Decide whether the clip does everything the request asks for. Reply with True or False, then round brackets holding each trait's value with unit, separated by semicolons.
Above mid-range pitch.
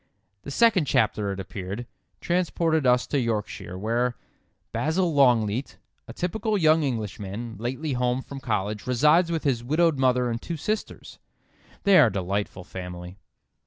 False (125 Hz)